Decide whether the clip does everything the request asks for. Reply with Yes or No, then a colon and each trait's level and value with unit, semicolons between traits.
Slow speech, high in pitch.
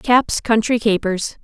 Yes: slow, 125 wpm; high, 220 Hz